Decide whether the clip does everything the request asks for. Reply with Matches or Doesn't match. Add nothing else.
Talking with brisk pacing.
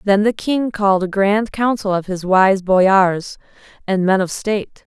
Doesn't match